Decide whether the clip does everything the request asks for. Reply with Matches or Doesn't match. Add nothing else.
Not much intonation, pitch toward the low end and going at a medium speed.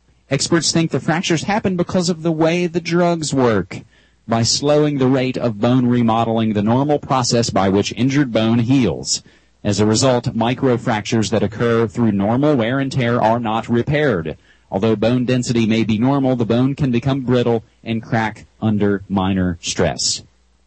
Doesn't match